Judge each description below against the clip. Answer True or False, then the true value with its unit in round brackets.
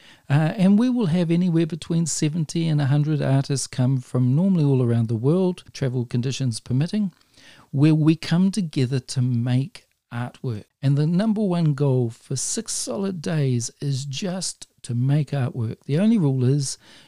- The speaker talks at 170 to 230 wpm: False (160 wpm)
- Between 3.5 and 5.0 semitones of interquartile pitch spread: True (4.7 semitones)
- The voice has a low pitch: False (145 Hz)